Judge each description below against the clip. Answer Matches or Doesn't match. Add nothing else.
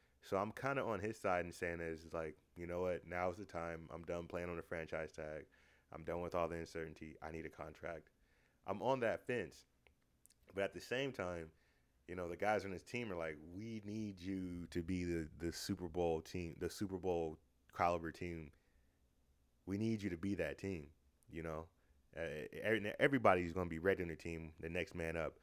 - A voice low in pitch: Matches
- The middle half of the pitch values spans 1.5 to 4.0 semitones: Matches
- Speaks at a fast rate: Matches